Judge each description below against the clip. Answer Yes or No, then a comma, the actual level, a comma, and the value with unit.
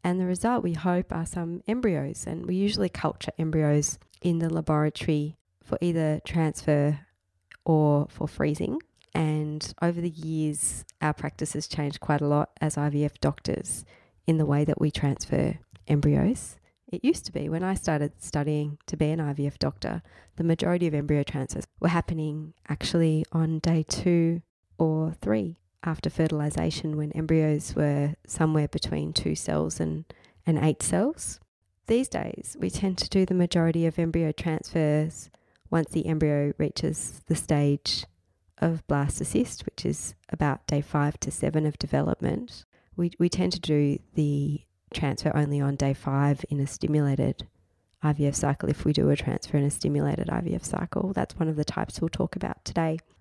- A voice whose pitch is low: No, medium, 155 Hz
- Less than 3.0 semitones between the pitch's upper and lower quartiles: Yes, narrow, 2.5 semitones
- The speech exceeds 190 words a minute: No, average, 165 wpm